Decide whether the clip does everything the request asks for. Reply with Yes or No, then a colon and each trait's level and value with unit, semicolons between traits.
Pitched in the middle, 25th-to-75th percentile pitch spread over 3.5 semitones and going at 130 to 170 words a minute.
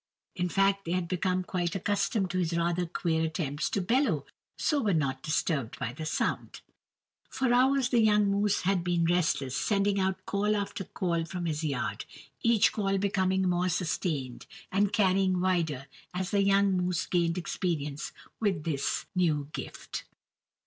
No: medium, 180 Hz; average, 3.2 semitones; average, 160 wpm